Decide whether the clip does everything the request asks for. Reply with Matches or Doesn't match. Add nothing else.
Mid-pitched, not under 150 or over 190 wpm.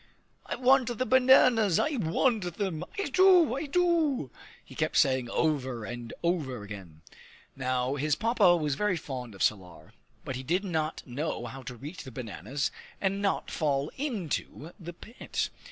Matches